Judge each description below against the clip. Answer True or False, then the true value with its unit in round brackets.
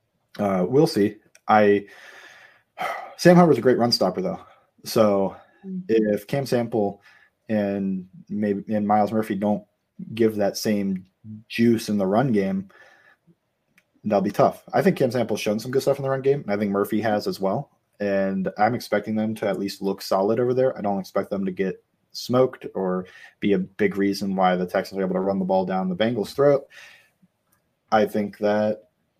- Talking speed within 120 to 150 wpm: False (185 wpm)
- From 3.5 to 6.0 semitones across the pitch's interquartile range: False (3.1 semitones)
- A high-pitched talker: False (105 Hz)